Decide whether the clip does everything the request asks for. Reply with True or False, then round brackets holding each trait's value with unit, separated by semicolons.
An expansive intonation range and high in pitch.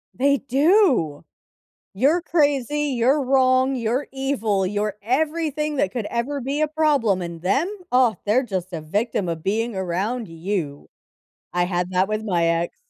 True (6.8 semitones; 235 Hz)